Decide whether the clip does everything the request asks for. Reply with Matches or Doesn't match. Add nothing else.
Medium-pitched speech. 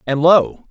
Matches